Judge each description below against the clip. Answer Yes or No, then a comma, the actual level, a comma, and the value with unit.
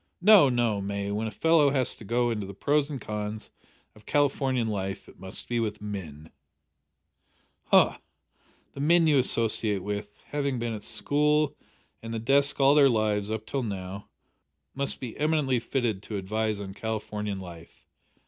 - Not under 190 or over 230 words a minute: No, average, 165 wpm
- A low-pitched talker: Yes, low, 110 Hz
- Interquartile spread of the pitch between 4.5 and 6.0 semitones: Yes, average, 5.1 semitones